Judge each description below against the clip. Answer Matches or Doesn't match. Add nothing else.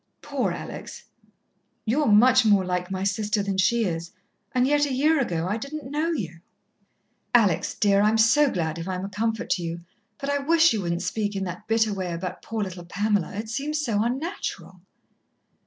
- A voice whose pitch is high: Matches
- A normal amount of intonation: Doesn't match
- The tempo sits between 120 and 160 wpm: Doesn't match